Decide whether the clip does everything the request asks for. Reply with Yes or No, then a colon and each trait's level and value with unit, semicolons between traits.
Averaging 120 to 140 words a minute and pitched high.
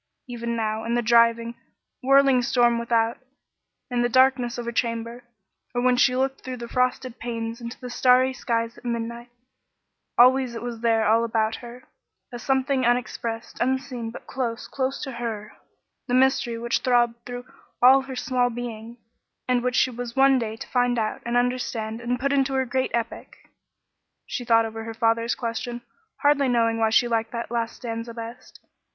No: average, 175 wpm; high, 240 Hz